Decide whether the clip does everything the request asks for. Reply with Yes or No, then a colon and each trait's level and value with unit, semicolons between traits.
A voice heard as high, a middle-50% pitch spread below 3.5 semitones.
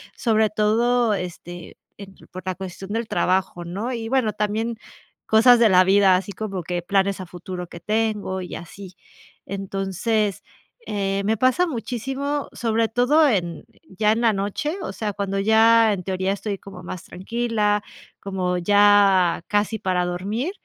Yes: high, 205 Hz; average, 3.1 semitones